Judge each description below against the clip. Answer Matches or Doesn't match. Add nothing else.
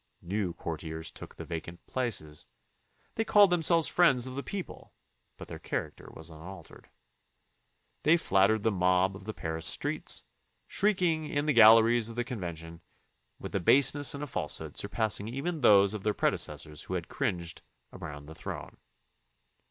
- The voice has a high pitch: Doesn't match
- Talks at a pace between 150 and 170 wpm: Matches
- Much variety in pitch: Matches